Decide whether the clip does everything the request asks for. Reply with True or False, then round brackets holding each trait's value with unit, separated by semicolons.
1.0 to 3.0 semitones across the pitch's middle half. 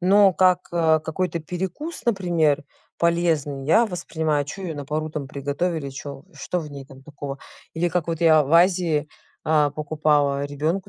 False (3.4 semitones)